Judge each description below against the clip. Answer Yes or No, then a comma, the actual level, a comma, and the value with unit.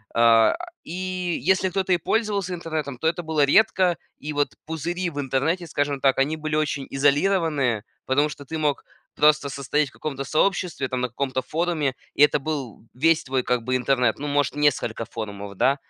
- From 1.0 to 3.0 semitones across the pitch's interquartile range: No, average, 3.8 semitones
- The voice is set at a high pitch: No, medium, 145 Hz